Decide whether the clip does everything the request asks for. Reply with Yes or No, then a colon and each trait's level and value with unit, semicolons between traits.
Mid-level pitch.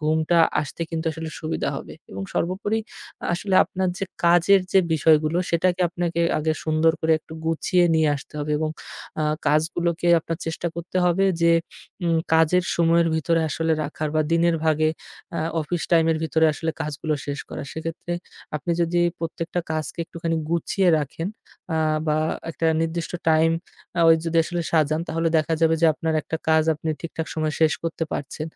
Yes: medium, 165 Hz